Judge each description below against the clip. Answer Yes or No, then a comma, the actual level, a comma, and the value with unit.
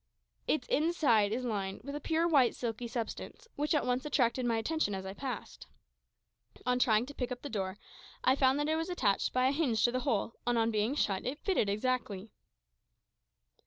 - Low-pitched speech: No, very high, 250 Hz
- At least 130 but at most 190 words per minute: No, average, 200 wpm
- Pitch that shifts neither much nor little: Yes, average, 4.6 semitones